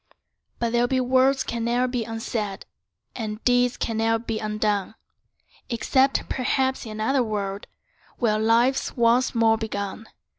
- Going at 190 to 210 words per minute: No, average, 140 wpm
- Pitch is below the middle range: No, high, 230 Hz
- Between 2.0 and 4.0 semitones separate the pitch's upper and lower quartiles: Yes, narrow, 2.4 semitones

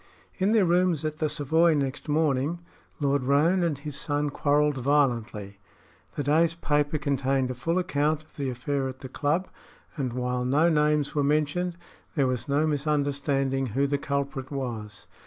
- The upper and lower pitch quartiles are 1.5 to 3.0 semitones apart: Yes, narrow, 2.4 semitones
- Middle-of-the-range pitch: Yes, medium, 145 Hz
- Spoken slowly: No, average, 165 wpm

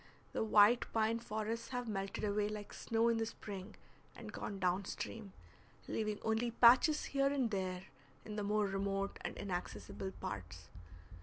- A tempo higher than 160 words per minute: No, average, 155 wpm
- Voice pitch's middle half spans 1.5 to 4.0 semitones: Yes, average, 2.8 semitones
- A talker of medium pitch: No, high, 210 Hz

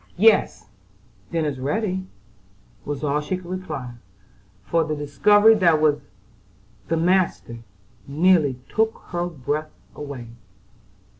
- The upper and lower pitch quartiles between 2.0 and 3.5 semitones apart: No, average, 4.3 semitones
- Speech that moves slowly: Yes, slow, 115 wpm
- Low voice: No, medium, 160 Hz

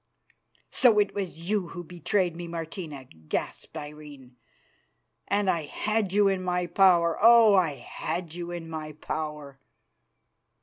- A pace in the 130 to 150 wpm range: Yes, slow, 135 wpm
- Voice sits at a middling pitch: Yes, medium, 170 Hz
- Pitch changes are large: No, average, 4.0 semitones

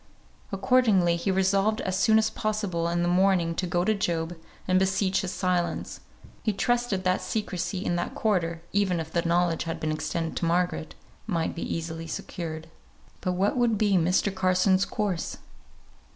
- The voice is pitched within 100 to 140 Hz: No, medium, 185 Hz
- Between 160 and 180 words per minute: Yes, average, 165 wpm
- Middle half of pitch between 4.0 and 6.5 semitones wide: No, average, 2.7 semitones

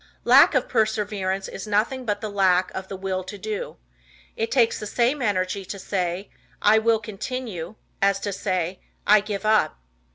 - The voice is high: Yes, high, 205 Hz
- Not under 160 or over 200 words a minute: Yes, average, 170 wpm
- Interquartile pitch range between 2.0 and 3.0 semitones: Yes, narrow, 2.6 semitones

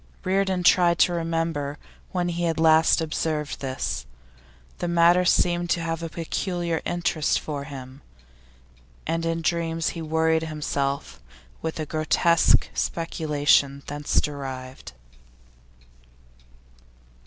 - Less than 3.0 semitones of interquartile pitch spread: Yes, narrow, 2.5 semitones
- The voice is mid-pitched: Yes, medium, 160 Hz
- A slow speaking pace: Yes, slow, 110 wpm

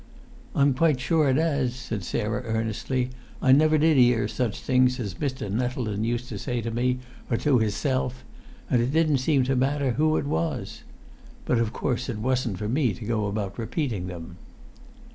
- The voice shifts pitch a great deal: No, average, 3.4 semitones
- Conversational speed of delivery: Yes, average, 180 wpm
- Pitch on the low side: Yes, low, 125 Hz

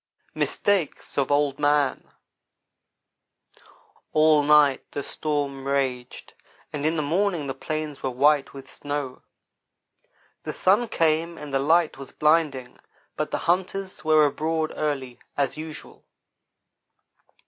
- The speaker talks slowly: Yes, slow, 120 wpm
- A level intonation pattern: Yes, narrow, 2.3 semitones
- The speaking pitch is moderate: Yes, medium, 150 Hz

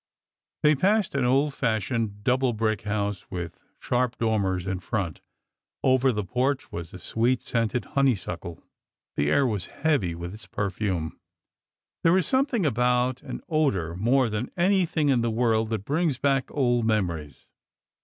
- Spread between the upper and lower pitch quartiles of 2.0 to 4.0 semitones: No, average, 5.2 semitones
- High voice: No, low, 115 Hz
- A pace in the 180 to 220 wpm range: No, average, 155 wpm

